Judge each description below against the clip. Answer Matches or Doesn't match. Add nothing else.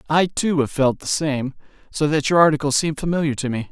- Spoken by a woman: Doesn't match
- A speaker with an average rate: Doesn't match